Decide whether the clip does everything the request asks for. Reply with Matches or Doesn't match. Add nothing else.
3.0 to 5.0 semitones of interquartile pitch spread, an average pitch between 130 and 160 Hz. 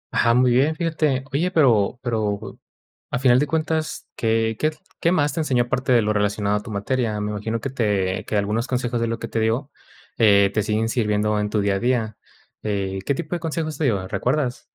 Doesn't match